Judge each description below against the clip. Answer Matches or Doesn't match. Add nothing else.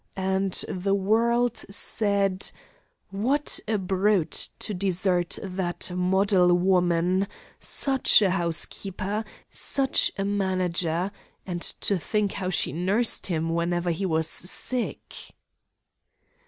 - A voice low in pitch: Doesn't match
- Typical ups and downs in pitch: Doesn't match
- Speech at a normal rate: Doesn't match